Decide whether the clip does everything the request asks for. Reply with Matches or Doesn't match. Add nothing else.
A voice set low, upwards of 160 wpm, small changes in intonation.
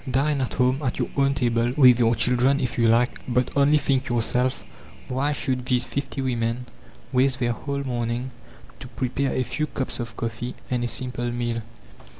Matches